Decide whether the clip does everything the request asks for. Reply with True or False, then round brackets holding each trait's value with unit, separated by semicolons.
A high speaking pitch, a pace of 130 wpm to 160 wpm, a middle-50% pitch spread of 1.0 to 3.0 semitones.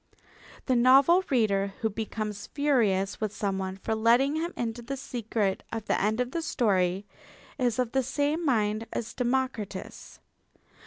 False (230 Hz; 150 wpm; 4.1 semitones)